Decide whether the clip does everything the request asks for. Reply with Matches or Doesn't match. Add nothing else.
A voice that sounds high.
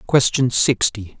Doesn't match